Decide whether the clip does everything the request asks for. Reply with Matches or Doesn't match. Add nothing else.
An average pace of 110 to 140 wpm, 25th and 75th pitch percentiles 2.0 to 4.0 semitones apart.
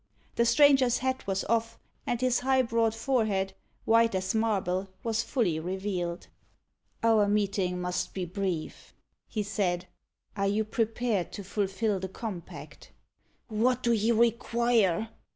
Matches